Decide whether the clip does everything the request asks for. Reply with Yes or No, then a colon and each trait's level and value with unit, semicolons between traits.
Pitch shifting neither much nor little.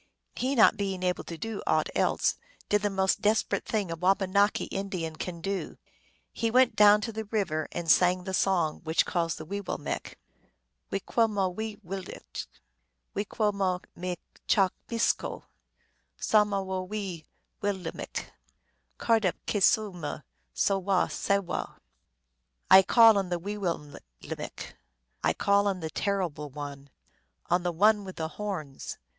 Yes: average, 3.3 semitones